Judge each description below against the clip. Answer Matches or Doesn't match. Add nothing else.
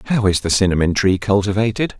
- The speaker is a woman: Doesn't match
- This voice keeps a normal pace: Matches